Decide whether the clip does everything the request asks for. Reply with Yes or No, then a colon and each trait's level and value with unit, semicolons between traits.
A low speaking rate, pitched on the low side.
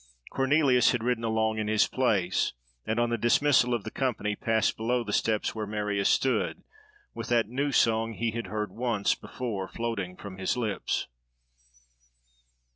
No: average, 160 wpm; low, 115 Hz